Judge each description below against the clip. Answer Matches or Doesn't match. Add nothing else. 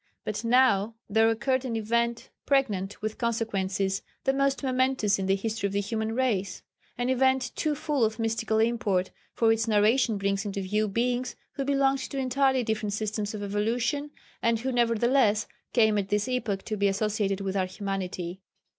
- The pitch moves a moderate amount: Matches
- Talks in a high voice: Matches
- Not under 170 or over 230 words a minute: Matches